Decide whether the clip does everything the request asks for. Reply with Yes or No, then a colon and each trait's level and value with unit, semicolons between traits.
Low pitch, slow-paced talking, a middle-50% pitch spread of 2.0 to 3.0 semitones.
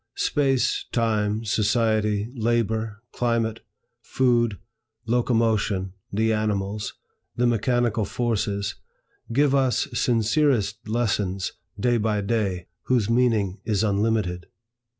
Yes: low, 110 Hz; slow, 90 wpm; narrow, 2.4 semitones